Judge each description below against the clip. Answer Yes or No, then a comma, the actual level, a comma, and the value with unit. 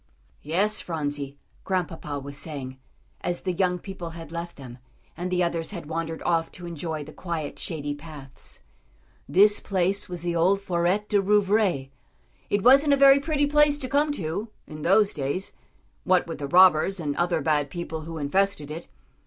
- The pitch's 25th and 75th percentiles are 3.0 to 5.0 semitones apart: Yes, average, 4.2 semitones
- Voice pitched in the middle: Yes, medium, 170 Hz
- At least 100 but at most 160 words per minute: No, average, 170 wpm